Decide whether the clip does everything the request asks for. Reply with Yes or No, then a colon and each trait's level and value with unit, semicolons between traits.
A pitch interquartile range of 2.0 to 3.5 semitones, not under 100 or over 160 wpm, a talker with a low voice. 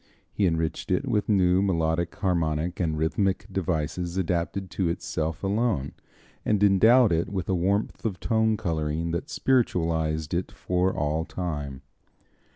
Yes: average, 3.2 semitones; average, 140 wpm; very low, 90 Hz